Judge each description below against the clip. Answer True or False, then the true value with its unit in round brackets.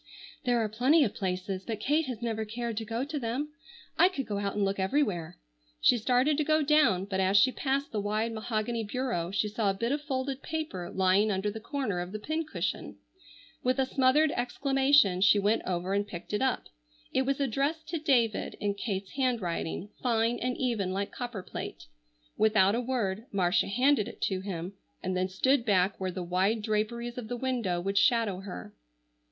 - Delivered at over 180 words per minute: True (190 wpm)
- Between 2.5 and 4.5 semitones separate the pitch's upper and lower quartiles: False (4.9 semitones)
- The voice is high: True (220 Hz)